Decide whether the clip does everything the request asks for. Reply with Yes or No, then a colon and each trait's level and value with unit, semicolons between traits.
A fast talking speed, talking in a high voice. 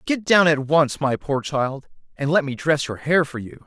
No: fast, 245 wpm; medium, 145 Hz